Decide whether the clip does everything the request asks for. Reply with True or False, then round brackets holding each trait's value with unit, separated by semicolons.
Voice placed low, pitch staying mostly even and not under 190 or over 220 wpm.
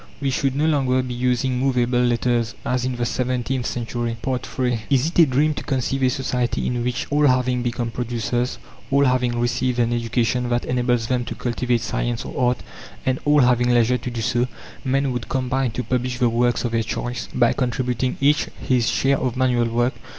True (125 Hz; 1.3 semitones; 195 wpm)